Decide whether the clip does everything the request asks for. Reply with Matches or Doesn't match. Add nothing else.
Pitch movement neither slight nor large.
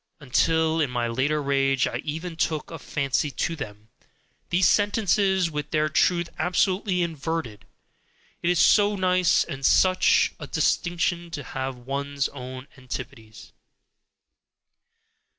Matches